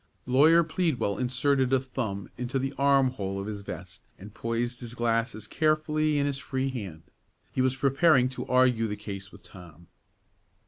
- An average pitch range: Yes, average, 4.7 semitones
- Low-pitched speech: Yes, low, 125 Hz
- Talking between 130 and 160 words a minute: No, average, 170 wpm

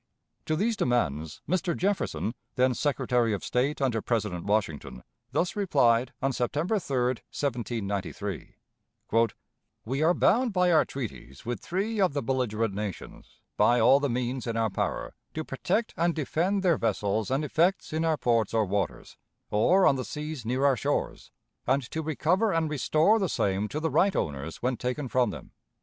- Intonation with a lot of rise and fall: Yes, wide, 6.1 semitones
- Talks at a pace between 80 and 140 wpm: No, average, 165 wpm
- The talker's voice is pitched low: Yes, low, 130 Hz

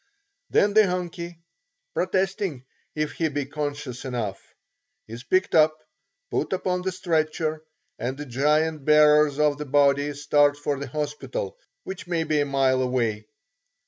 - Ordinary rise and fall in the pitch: Yes, average, 3.1 semitones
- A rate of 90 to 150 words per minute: Yes, average, 145 wpm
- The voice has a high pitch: No, medium, 150 Hz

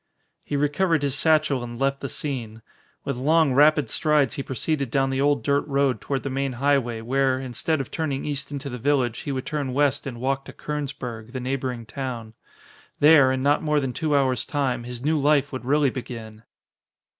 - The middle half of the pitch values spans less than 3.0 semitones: Yes, narrow, 2.4 semitones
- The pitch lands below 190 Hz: Yes, low, 135 Hz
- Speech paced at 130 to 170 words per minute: No, average, 195 wpm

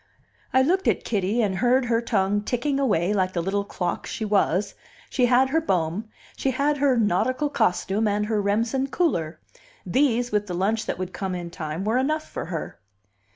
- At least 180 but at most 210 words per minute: Yes, average, 190 wpm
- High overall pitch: Yes, high, 215 Hz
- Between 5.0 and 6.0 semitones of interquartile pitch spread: Yes, average, 5.3 semitones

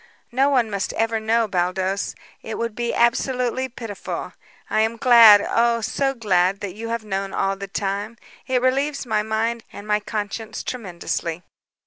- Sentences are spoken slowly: No, average, 160 wpm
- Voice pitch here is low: No, high, 220 Hz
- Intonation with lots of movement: No, average, 2.9 semitones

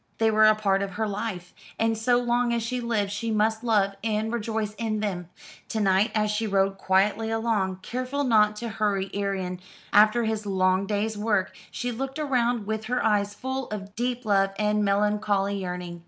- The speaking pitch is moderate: No, high, 215 Hz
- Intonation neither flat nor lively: No, narrow, 2.3 semitones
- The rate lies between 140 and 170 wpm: No, average, 185 wpm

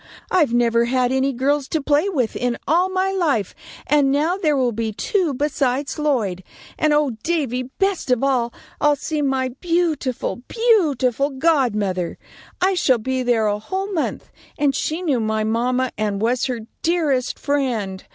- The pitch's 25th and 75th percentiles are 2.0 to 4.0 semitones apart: No, average, 4.4 semitones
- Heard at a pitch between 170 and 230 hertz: No, very high, 270 Hz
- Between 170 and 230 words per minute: No, average, 160 wpm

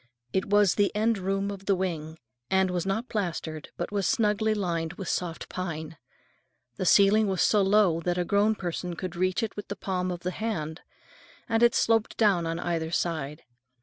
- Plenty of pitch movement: No, average, 3.3 semitones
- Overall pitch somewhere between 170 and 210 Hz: Yes, high, 190 Hz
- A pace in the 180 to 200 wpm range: Yes, average, 190 wpm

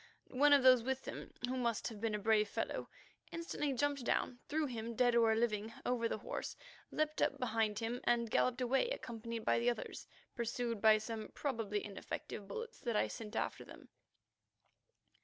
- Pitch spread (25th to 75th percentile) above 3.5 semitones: No, narrow, 2.6 semitones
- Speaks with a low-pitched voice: No, high, 235 Hz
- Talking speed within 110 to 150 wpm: No, average, 175 wpm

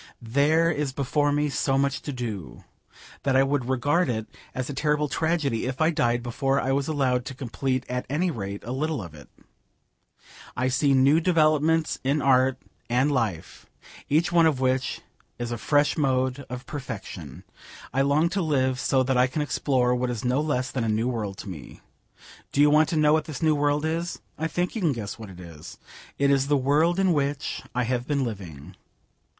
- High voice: No, low, 135 Hz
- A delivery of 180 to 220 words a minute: Yes, average, 200 wpm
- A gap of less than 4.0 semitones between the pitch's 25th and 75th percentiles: Yes, average, 3.2 semitones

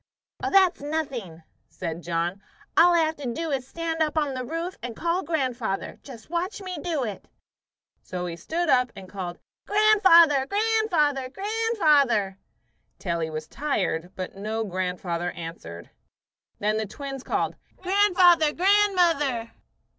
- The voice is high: Yes, very high, 275 Hz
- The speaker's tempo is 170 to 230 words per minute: No, average, 145 wpm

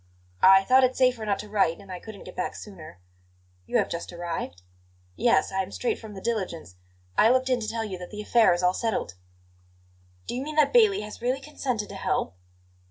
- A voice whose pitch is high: Yes, high, 210 Hz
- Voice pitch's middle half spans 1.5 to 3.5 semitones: No, average, 5.2 semitones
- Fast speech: Yes, fast, 215 wpm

